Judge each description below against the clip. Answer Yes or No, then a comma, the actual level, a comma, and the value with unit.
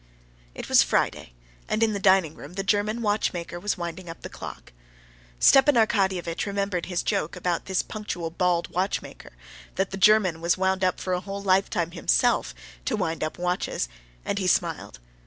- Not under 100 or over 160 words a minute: No, average, 175 wpm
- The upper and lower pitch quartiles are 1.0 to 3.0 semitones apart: Yes, average, 2.7 semitones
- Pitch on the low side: No, medium, 185 Hz